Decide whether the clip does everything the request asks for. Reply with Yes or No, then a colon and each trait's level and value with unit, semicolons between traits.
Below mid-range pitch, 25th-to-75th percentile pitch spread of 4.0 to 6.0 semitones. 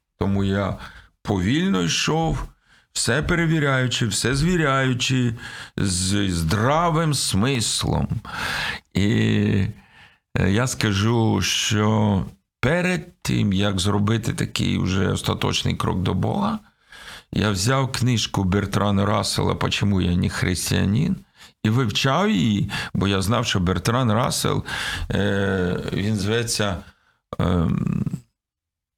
Yes: low, 110 Hz; average, 5.0 semitones